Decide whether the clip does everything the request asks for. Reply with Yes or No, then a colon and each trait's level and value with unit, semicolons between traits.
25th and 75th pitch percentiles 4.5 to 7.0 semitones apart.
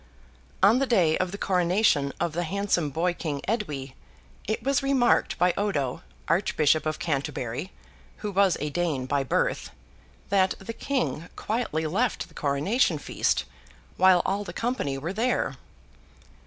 Yes: wide, 5.6 semitones